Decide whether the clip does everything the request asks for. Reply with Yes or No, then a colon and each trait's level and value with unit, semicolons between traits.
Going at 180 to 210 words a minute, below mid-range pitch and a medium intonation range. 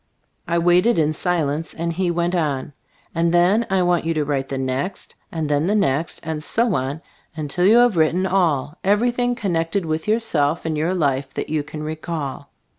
No: average, 190 wpm; medium, 165 Hz; average, 3.5 semitones